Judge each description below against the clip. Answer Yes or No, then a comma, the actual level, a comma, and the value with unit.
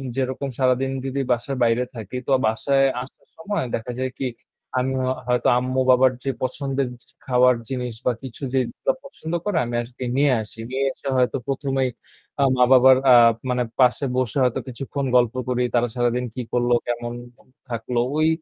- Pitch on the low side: Yes, low, 130 Hz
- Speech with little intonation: Yes, narrow, 1.6 semitones